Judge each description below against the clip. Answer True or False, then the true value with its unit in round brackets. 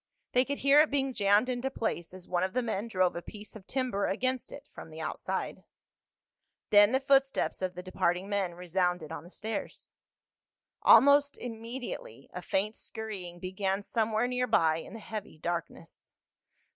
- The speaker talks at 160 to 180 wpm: True (170 wpm)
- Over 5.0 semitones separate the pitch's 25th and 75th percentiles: True (5.4 semitones)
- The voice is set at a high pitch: True (210 Hz)